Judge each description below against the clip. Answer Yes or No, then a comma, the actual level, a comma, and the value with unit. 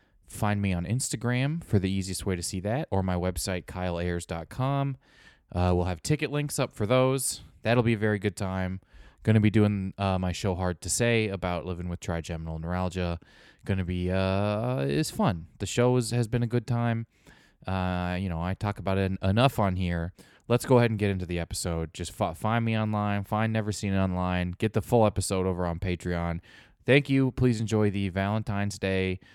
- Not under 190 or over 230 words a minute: Yes, average, 200 wpm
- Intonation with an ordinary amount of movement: Yes, average, 3.6 semitones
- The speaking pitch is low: Yes, very low, 95 Hz